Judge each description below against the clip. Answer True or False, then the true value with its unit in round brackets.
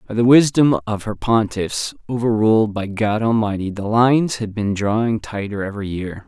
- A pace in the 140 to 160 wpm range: False (180 wpm)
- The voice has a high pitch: False (110 Hz)